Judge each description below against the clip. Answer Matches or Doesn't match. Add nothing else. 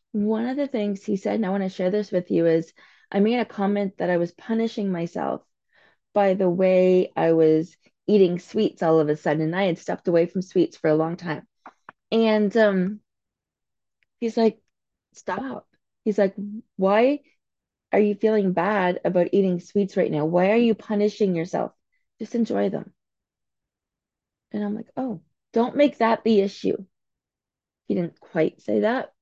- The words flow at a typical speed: Matches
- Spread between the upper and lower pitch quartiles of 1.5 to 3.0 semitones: Doesn't match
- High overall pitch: Matches